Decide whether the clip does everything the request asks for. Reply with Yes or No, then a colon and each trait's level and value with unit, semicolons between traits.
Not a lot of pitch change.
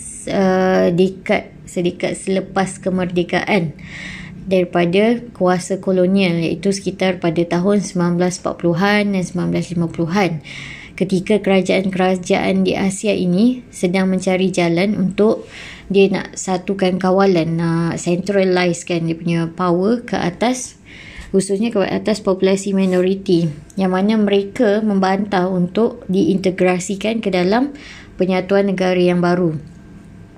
Yes: narrow, 1.8 semitones